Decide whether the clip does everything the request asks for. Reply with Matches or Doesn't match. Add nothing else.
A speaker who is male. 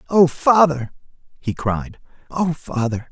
Matches